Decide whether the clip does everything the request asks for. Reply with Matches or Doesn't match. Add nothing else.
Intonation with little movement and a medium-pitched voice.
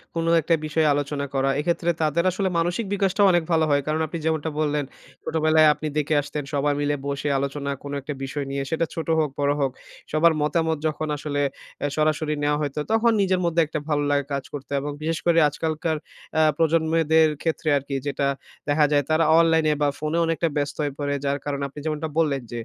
Matches